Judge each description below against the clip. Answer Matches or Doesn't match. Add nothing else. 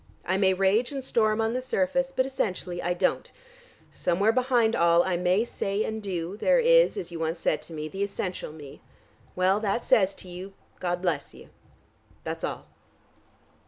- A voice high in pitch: Matches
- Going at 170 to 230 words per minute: Matches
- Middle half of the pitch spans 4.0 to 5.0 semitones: Matches